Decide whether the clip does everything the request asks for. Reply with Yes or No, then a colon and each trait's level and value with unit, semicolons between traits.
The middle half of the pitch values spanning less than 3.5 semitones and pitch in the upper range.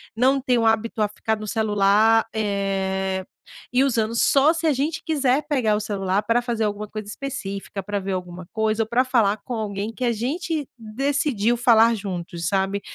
No: average, 3.8 semitones; high, 220 Hz